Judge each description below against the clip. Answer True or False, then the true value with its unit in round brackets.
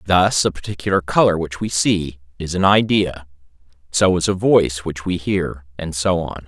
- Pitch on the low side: True (85 Hz)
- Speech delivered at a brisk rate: False (185 wpm)